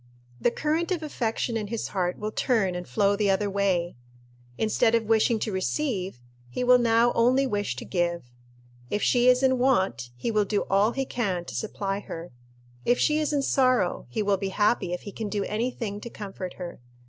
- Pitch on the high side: Yes, high, 210 Hz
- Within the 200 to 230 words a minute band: Yes, fast, 205 wpm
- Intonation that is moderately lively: Yes, average, 4.1 semitones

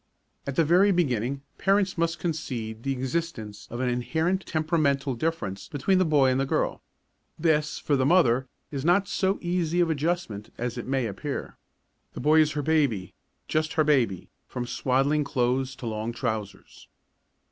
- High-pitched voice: No, medium, 140 Hz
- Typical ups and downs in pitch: Yes, average, 4.9 semitones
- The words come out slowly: No, average, 165 wpm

